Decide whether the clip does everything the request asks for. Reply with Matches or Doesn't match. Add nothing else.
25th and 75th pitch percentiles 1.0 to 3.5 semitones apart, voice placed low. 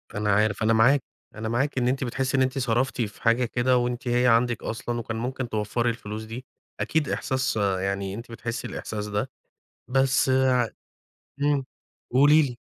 Matches